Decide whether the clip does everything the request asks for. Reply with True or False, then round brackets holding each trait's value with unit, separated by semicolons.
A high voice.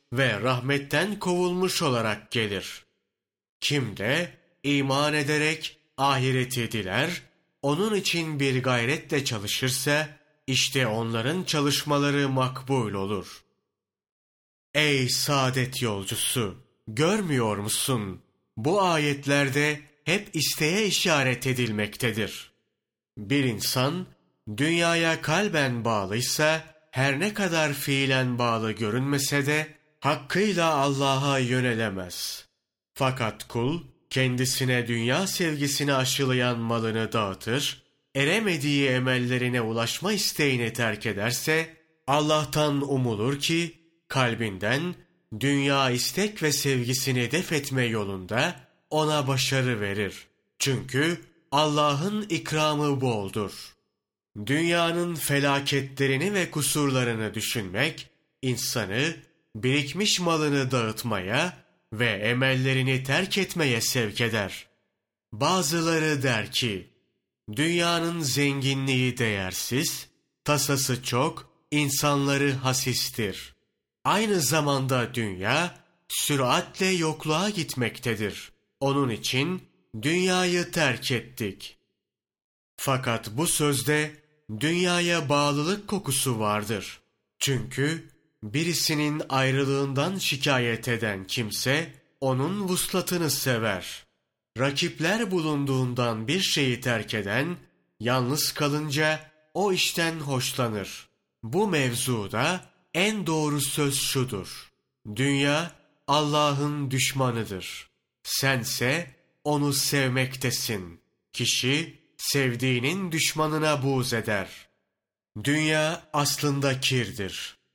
False (140 Hz)